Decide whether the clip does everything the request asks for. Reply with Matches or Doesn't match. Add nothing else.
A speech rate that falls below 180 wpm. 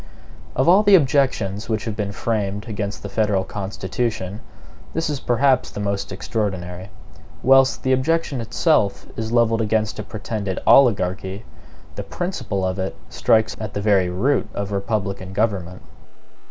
Matches